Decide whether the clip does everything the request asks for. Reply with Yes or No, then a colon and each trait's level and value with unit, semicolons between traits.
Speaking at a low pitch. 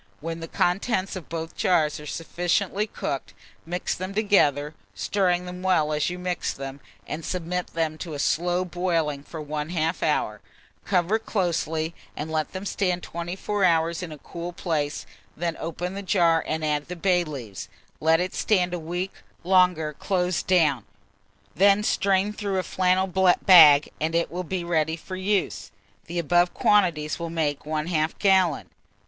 No: medium, 175 Hz